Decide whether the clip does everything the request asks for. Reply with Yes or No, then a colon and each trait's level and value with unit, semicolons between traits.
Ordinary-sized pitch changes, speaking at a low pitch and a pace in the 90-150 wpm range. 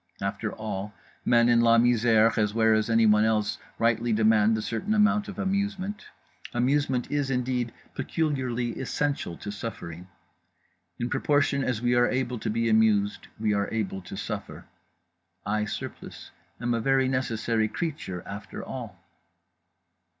Yes: average, 3.4 semitones; low, 115 Hz; average, 145 wpm